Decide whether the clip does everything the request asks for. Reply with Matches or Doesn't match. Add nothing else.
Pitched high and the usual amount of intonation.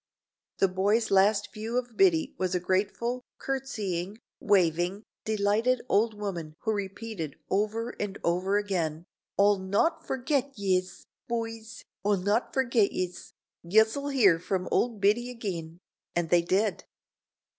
Matches